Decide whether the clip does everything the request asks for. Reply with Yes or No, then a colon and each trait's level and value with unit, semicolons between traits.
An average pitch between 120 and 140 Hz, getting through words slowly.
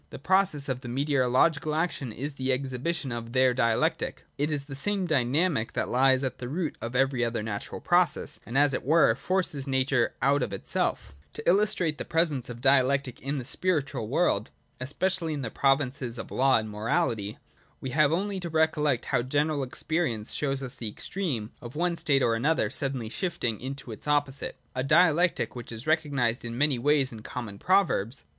No: low, 135 Hz; average, 185 wpm